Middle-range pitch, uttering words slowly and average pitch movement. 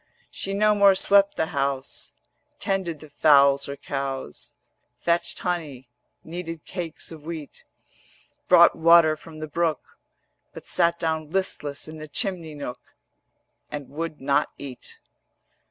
Yes: medium, 160 Hz; slow, 130 wpm; average, 3.3 semitones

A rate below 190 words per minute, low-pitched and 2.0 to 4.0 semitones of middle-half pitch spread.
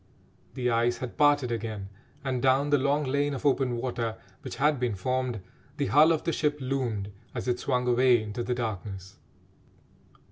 Yes: average, 175 wpm; low, 125 Hz; average, 3.2 semitones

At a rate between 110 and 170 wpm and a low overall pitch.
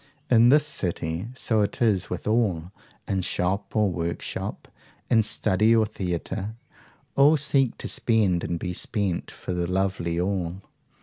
Yes: average, 145 wpm; low, 100 Hz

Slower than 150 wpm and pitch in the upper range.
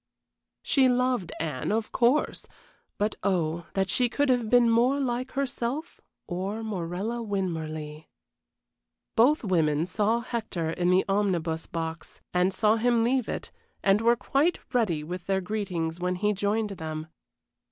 Yes: average, 140 wpm; high, 205 Hz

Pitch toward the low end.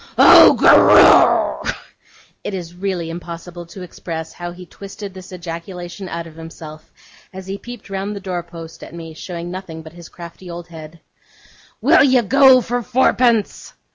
No: medium, 175 Hz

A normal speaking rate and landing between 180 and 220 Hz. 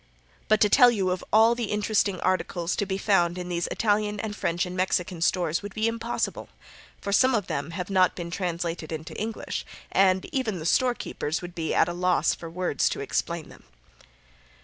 Yes: average, 195 wpm; medium, 185 Hz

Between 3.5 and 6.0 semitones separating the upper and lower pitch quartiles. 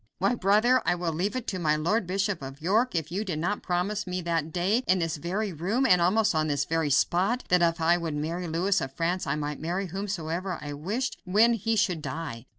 Yes: average, 3.8 semitones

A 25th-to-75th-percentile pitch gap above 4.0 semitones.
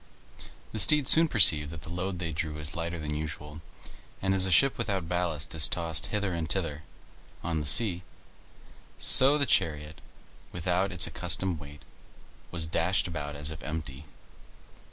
No: average, 3.7 semitones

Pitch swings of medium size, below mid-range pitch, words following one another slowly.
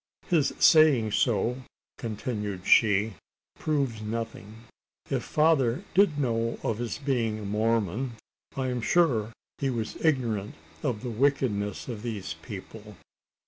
Yes: average, 3.9 semitones; low, 115 Hz; slow, 125 wpm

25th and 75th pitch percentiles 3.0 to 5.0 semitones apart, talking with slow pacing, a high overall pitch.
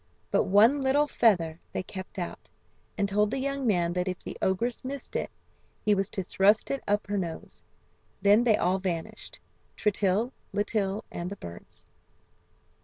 No: average, 3.7 semitones; average, 165 wpm; high, 205 Hz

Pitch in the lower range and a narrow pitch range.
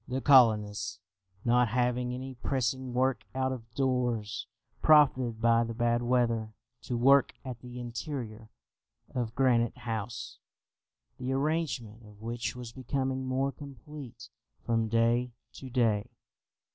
Yes: low, 125 Hz; narrow, 2.2 semitones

